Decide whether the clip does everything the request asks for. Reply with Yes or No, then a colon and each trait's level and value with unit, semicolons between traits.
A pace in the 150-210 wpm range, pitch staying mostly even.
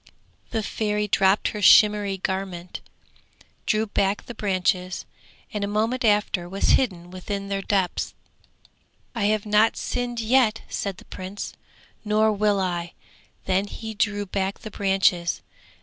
No: slow, 135 wpm; narrow, 2.0 semitones